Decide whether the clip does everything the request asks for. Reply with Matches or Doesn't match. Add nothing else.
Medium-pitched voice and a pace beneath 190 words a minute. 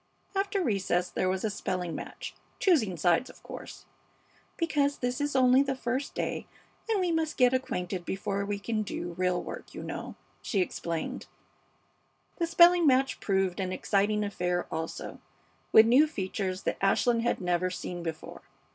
Doesn't match